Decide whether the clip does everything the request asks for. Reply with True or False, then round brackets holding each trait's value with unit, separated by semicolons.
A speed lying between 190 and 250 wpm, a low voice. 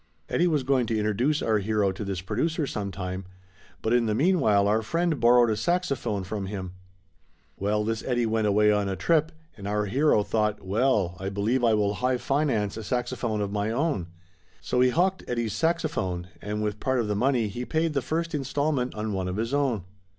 True (200 wpm; 110 Hz)